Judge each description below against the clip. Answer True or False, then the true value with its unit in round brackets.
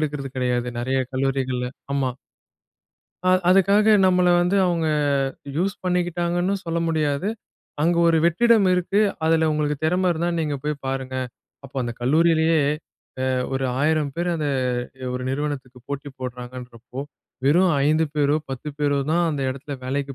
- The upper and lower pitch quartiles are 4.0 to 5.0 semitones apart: True (4.4 semitones)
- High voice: False (150 Hz)